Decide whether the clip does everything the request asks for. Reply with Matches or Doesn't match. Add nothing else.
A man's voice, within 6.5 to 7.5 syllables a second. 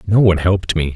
Matches